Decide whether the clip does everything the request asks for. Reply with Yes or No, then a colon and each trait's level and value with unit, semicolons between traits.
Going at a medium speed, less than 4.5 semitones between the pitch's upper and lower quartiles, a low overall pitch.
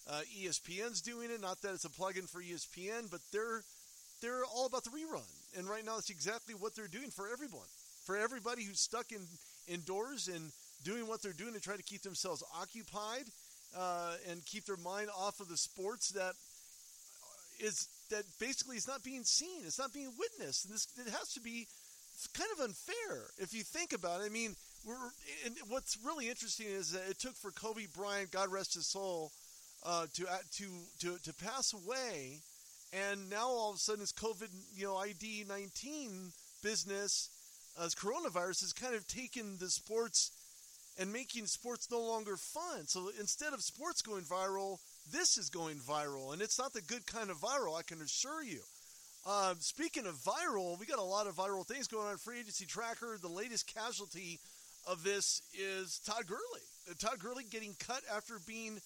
No: average, 190 wpm; average, 4.0 semitones; high, 210 Hz